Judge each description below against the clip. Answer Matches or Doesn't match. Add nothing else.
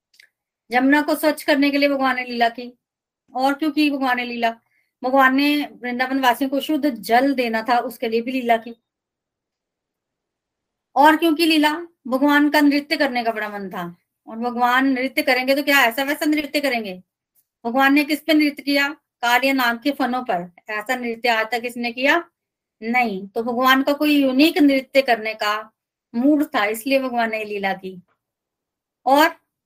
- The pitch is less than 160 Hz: Doesn't match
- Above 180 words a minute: Doesn't match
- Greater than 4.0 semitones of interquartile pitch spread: Doesn't match